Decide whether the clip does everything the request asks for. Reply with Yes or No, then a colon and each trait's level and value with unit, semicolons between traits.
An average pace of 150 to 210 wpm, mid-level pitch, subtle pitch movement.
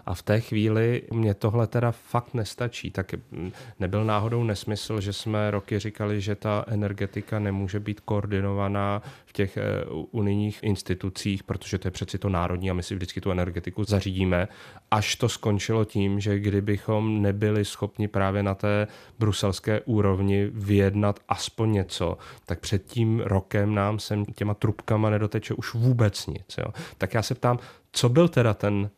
No: average, 160 wpm; low, 105 Hz; narrow, 1.8 semitones